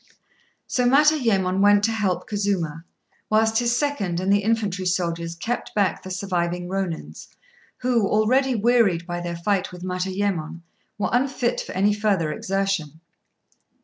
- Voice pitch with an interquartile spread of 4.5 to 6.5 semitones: No, average, 3.9 semitones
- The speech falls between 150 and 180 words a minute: No, average, 140 wpm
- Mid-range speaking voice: No, high, 195 Hz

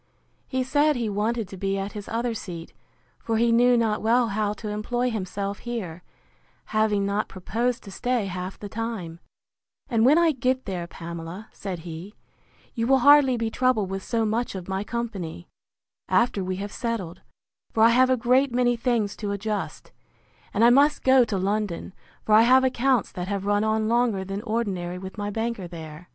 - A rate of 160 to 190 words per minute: Yes, average, 185 wpm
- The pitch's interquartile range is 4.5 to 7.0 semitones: No, average, 3.7 semitones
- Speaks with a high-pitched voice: Yes, high, 215 Hz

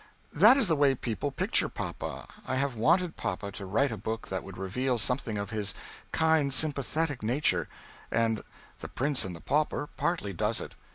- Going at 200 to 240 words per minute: No, average, 180 wpm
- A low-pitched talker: Yes, low, 125 Hz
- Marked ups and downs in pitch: Yes, wide, 5.8 semitones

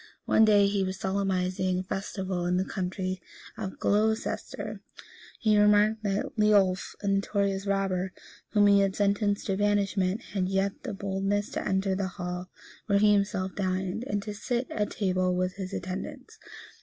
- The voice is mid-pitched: No, high, 195 Hz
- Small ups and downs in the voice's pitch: Yes, narrow, 1.6 semitones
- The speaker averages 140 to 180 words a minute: Yes, average, 165 wpm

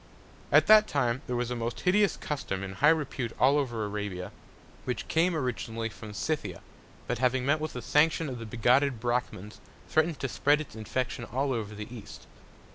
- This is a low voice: Yes, low, 125 Hz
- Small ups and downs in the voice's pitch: No, average, 4.6 semitones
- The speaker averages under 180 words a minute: No, average, 185 wpm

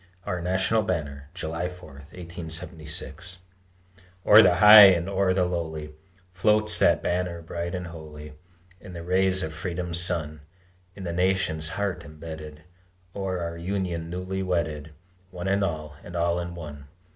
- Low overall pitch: Yes, very low, 85 Hz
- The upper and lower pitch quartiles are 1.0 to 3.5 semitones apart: Yes, average, 2.7 semitones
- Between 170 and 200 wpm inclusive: No, average, 145 wpm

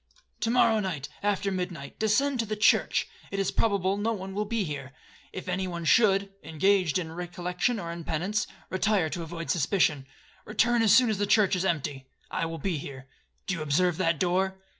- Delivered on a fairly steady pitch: No, average, 3.8 semitones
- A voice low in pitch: No, medium, 185 Hz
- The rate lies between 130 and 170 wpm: No, average, 195 wpm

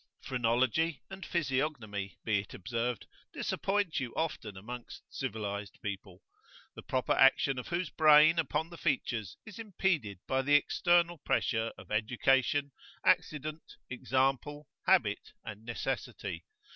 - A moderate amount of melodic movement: No, wide, 5.8 semitones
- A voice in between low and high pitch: No, low, 130 Hz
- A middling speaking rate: No, slow, 120 wpm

